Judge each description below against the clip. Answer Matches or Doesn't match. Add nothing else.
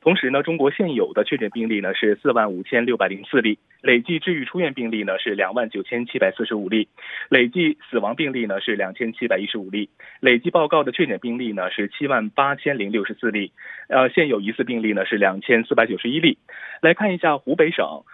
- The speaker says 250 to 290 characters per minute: Doesn't match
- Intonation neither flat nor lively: Matches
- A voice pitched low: Matches